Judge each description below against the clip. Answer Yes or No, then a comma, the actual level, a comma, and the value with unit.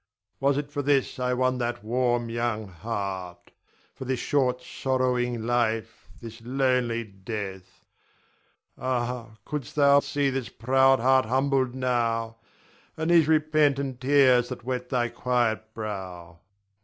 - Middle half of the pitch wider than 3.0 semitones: No, average, 2.7 semitones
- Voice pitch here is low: Yes, low, 125 Hz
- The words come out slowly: Yes, slow, 130 wpm